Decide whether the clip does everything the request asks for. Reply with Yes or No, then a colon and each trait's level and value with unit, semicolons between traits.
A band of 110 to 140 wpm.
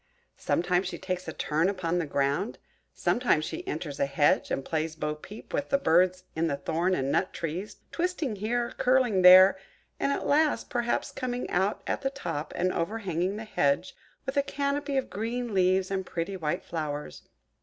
No: average, 180 wpm